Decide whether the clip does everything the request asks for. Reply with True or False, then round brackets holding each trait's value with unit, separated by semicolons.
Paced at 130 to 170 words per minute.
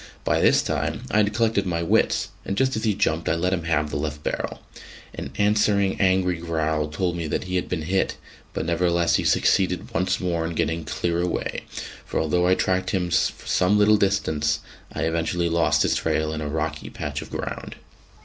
False (200 wpm)